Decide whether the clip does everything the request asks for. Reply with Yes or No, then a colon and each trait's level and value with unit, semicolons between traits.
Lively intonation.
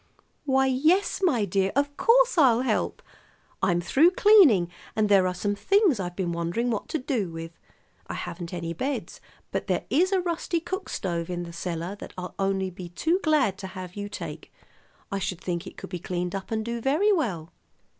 Yes: wide, 8.8 semitones